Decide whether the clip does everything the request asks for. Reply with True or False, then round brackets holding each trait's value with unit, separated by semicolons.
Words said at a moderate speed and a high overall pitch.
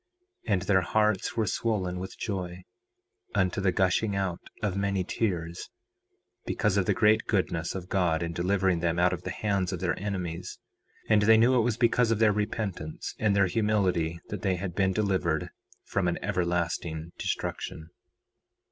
False (170 wpm; 95 Hz)